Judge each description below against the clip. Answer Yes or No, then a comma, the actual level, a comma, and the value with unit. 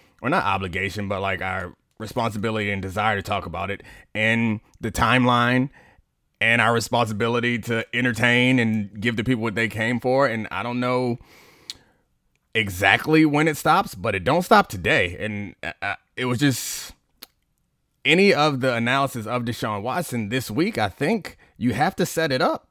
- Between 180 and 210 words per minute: No, average, 170 wpm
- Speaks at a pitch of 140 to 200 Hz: No, low, 115 Hz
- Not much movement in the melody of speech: No, average, 3.4 semitones